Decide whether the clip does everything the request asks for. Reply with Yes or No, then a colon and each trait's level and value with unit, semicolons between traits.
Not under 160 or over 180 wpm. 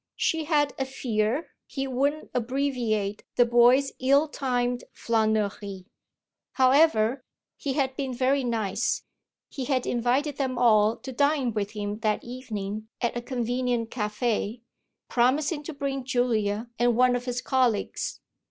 No: slow, 135 wpm